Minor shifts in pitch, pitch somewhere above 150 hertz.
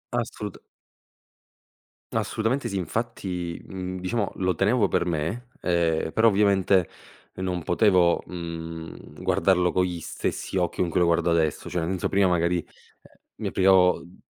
No: narrow, 2.2 semitones; very low, 90 Hz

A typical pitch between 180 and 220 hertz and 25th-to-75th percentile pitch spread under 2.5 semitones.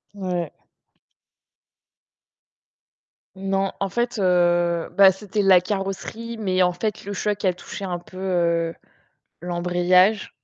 Yes: medium, 185 Hz; narrow, 2.1 semitones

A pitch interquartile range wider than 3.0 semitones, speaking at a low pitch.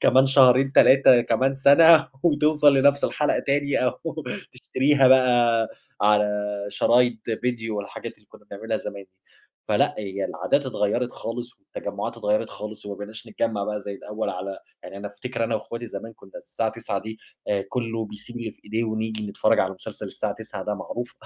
Yes: average, 3.5 semitones; low, 115 Hz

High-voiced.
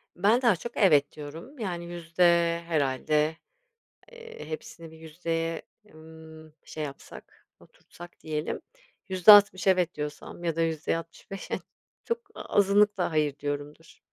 No: medium, 165 Hz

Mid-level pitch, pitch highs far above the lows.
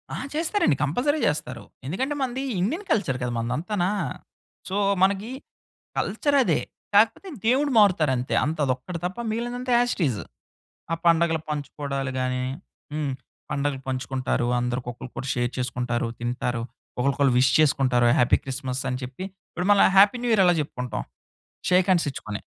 Yes: medium, 145 Hz; wide, 8.0 semitones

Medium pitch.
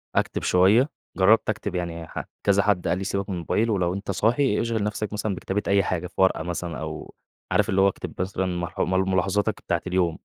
No: very low, 95 Hz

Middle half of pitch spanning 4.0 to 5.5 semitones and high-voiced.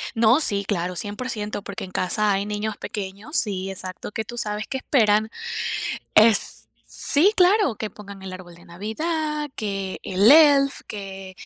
Yes: average, 4.6 semitones; high, 210 Hz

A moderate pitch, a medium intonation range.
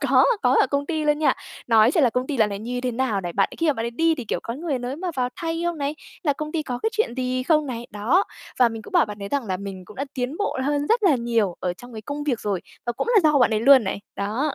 No: very high, 255 Hz; average, 5.0 semitones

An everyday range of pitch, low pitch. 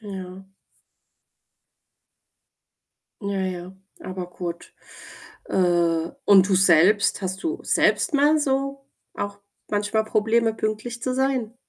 No: average, 4.3 semitones; high, 205 Hz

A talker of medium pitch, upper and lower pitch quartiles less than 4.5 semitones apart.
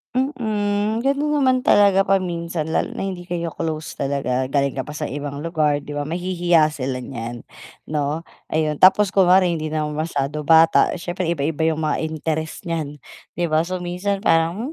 Yes: medium, 165 Hz; average, 3.6 semitones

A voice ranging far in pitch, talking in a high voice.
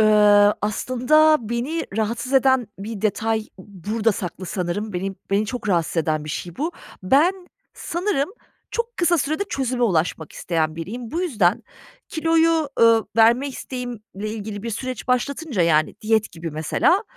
Yes: wide, 5.9 semitones; high, 225 Hz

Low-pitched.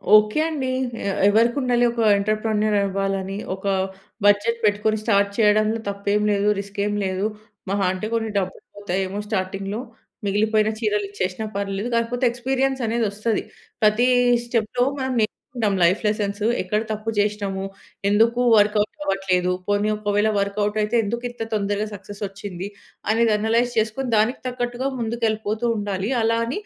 No: high, 210 Hz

